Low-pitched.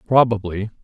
Yes: low, 110 Hz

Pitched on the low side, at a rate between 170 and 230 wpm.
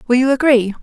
No: very high, 250 Hz; fast, 220 wpm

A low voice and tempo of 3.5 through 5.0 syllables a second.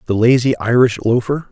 No: low, 120 Hz; 5.3 syllables/s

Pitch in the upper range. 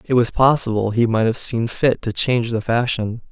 No: low, 115 Hz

